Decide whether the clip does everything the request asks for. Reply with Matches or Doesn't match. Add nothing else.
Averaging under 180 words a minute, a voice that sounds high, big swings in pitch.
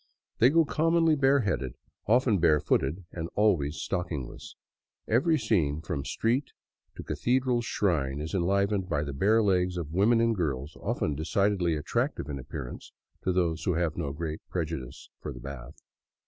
Doesn't match